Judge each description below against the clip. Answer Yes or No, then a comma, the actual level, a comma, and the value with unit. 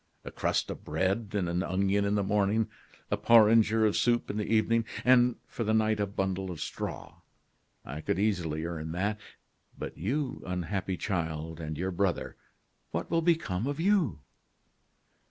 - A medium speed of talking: Yes, average, 165 wpm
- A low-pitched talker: Yes, low, 100 Hz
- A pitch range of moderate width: Yes, average, 4.0 semitones